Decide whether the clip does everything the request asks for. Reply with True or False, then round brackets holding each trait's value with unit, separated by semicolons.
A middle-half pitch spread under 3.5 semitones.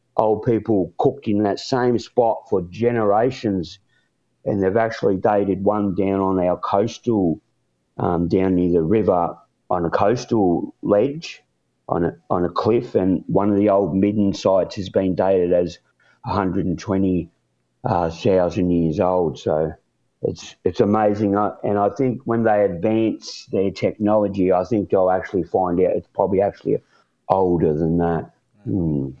True (2.8 semitones)